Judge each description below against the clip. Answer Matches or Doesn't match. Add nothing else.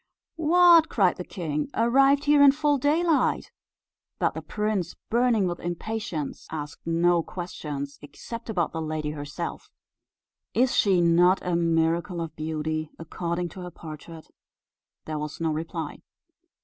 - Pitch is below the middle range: Doesn't match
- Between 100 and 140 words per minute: Matches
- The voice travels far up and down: Matches